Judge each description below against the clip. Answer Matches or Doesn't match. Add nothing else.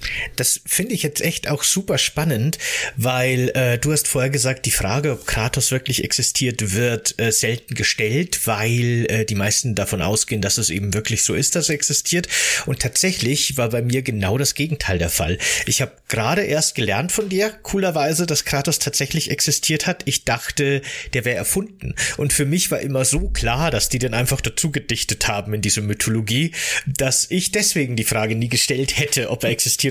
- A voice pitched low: Matches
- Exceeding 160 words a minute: Matches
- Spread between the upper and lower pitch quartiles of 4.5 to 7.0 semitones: Matches